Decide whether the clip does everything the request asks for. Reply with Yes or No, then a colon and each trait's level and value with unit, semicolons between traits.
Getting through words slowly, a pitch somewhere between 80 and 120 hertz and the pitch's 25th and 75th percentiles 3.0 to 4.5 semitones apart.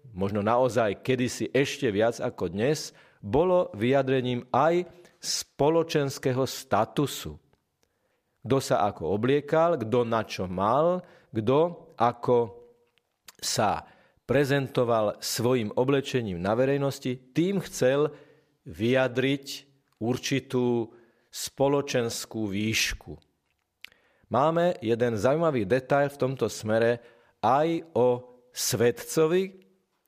No: slow, 90 wpm; low, 130 Hz; average, 3.3 semitones